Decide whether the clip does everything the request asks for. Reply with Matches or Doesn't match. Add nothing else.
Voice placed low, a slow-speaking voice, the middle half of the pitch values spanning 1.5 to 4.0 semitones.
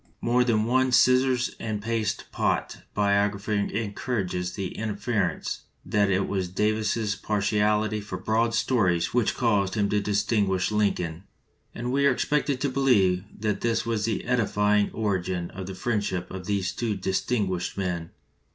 Doesn't match